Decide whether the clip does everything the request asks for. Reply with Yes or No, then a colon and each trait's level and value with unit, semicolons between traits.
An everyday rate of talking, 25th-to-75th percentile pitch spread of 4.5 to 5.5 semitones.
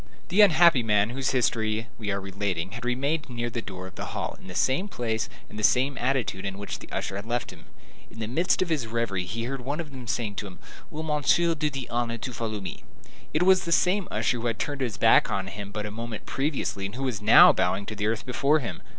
No: fast, 250 wpm; average, 4.8 semitones